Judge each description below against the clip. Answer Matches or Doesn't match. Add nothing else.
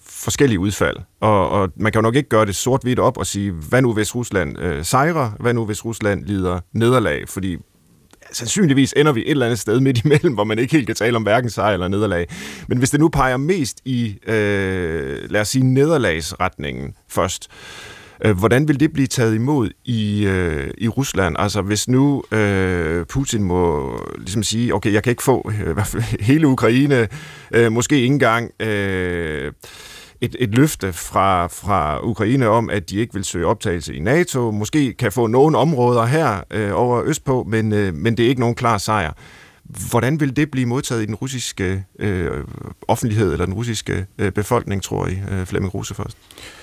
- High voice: Doesn't match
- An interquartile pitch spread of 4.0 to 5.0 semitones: Matches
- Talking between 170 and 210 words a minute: Matches